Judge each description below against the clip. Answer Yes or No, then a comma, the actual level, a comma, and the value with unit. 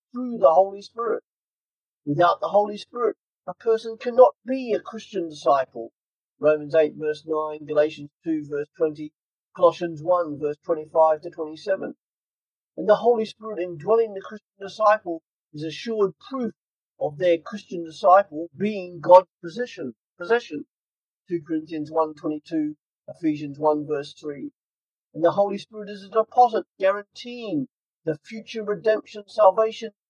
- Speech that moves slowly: Yes, slow, 130 wpm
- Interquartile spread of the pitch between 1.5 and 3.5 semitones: No, wide, 5.6 semitones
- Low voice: No, medium, 180 Hz